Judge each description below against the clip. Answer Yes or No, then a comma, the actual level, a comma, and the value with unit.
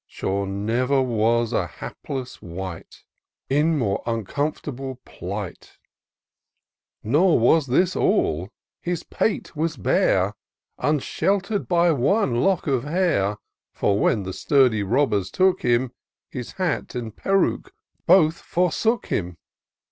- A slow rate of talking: Yes, slow, 115 wpm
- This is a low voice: Yes, low, 130 Hz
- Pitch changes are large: Yes, wide, 8.0 semitones